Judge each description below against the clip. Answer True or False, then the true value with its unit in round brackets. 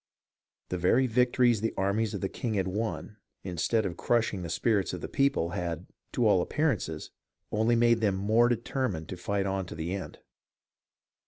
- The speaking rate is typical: True (185 wpm)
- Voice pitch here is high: False (100 Hz)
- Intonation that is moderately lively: True (4.4 semitones)